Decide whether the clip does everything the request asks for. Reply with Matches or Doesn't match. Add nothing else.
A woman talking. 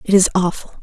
Matches